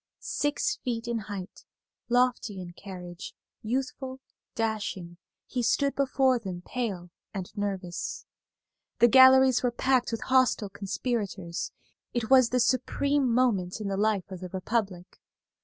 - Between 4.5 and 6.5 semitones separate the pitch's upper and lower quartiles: Yes, average, 5.0 semitones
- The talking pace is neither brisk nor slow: No, slow, 130 wpm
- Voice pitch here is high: Yes, high, 225 Hz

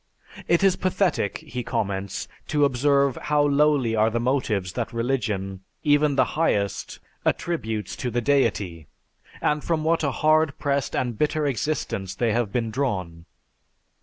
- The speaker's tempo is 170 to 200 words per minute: No, average, 145 wpm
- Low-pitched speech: Yes, low, 130 Hz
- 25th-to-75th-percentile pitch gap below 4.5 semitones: No, wide, 5.6 semitones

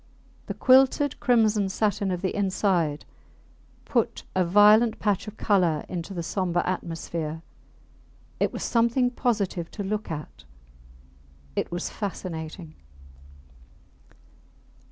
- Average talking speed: No, slow, 110 wpm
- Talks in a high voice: Yes, high, 195 Hz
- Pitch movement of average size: Yes, average, 4.0 semitones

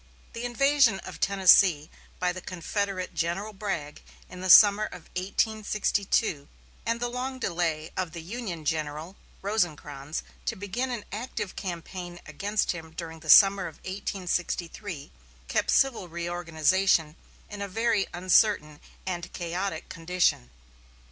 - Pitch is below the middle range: No, medium, 185 Hz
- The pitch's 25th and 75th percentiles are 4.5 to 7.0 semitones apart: No, average, 3.8 semitones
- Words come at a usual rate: No, slow, 130 wpm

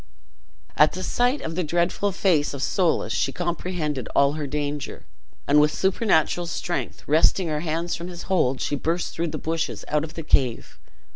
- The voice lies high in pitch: No, medium, 160 Hz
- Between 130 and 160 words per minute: No, average, 180 wpm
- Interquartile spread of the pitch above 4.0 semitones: No, average, 2.9 semitones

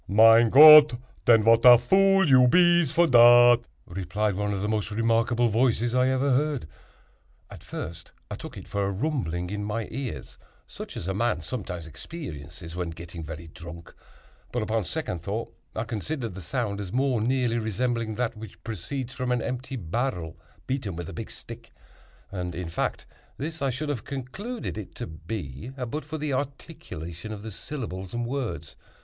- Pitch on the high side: No, low, 115 Hz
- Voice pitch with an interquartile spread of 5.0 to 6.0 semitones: Yes, wide, 5.6 semitones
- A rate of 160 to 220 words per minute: Yes, average, 170 wpm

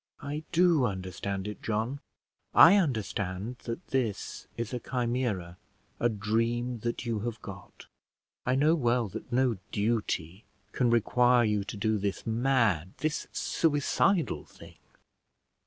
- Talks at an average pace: No, slow, 130 wpm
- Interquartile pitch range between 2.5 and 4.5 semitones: Yes, average, 3.7 semitones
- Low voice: Yes, low, 115 Hz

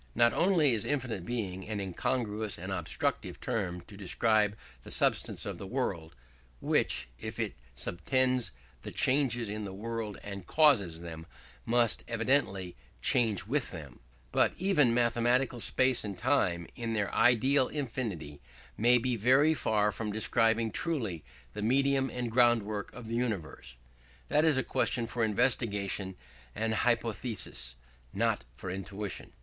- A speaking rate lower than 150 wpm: Yes, average, 140 wpm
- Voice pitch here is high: No, low, 115 Hz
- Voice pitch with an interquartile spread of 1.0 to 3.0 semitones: No, average, 4.1 semitones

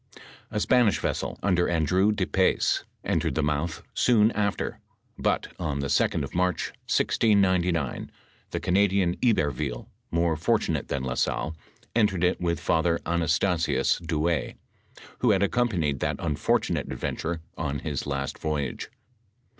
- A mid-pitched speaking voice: No, very low, 85 Hz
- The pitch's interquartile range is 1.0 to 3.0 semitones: No, average, 4.3 semitones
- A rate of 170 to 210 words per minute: No, average, 140 wpm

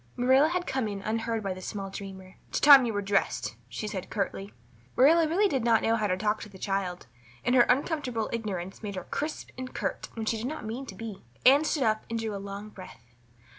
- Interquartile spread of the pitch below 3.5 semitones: No, average, 4.6 semitones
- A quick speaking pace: Yes, fast, 230 wpm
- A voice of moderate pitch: No, high, 220 Hz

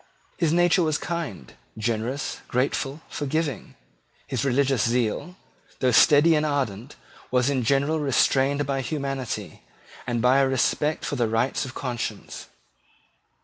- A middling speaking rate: No, slow, 130 wpm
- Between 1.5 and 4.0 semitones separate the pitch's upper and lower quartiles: Yes, average, 3.2 semitones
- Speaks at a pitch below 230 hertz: Yes, low, 135 Hz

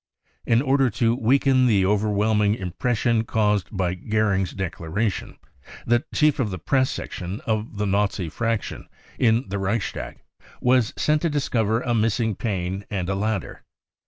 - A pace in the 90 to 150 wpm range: Yes, average, 145 wpm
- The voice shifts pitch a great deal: No, average, 3.4 semitones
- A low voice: Yes, low, 110 Hz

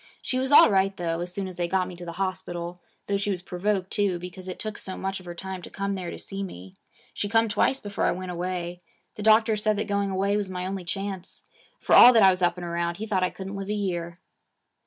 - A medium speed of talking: No, fast, 260 wpm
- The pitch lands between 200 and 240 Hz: No, high, 190 Hz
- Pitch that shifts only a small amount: Yes, narrow, 2.2 semitones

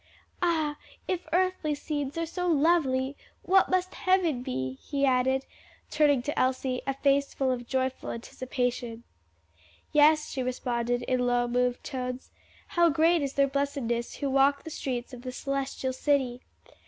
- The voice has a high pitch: Yes, very high, 270 Hz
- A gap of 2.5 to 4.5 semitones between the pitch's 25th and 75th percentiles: Yes, average, 3.2 semitones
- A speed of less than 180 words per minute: Yes, average, 150 wpm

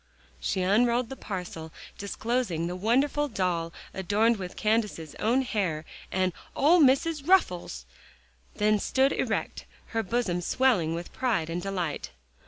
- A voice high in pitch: Yes, high, 205 Hz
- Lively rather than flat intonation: Yes, wide, 5.8 semitones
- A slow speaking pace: Yes, slow, 130 wpm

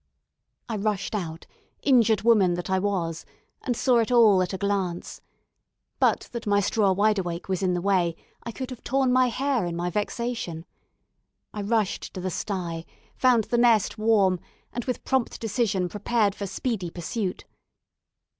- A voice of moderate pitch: No, high, 205 Hz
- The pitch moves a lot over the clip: No, average, 4.3 semitones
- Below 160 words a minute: No, average, 165 wpm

